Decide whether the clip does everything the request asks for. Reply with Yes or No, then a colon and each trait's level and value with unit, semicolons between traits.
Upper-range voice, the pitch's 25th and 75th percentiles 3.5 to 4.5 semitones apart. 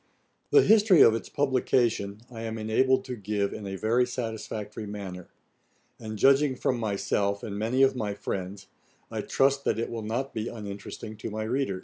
No: low, 110 Hz; average, 3.9 semitones